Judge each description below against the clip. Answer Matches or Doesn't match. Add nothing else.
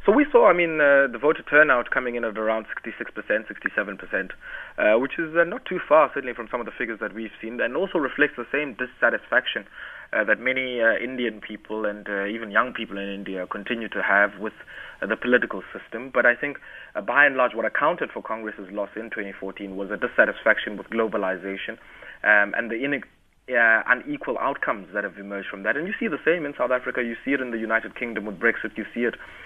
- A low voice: Matches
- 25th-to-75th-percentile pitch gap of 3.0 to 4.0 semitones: Matches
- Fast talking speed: Matches